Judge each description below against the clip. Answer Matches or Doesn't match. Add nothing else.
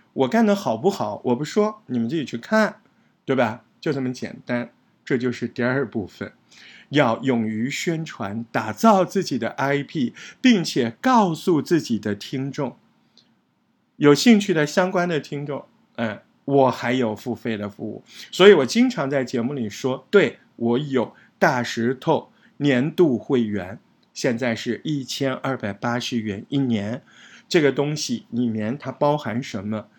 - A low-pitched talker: Matches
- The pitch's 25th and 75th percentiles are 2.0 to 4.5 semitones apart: Doesn't match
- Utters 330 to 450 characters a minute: Doesn't match